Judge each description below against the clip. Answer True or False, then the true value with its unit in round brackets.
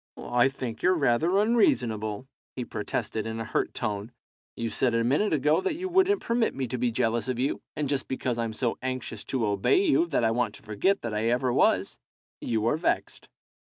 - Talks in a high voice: False (125 Hz)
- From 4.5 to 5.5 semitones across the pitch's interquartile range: True (5.1 semitones)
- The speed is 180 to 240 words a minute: True (205 wpm)